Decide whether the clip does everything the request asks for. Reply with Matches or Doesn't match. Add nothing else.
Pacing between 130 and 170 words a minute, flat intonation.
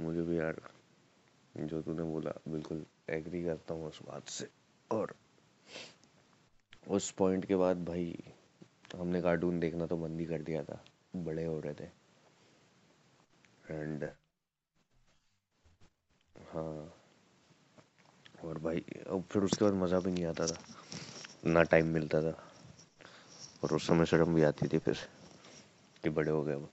Matches